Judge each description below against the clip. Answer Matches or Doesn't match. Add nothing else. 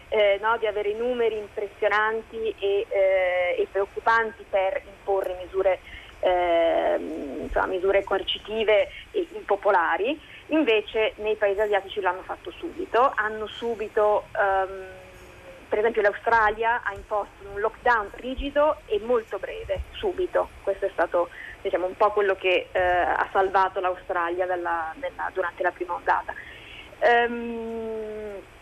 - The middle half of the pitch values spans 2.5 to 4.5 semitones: Matches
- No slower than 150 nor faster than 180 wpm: Doesn't match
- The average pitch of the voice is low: Doesn't match